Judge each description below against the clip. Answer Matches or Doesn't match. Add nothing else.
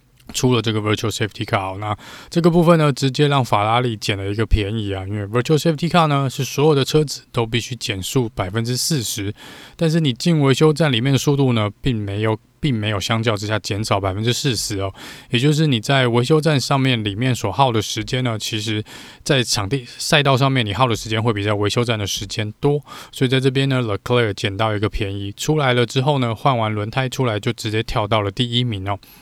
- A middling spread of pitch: Matches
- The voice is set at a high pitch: Doesn't match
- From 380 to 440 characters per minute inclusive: Matches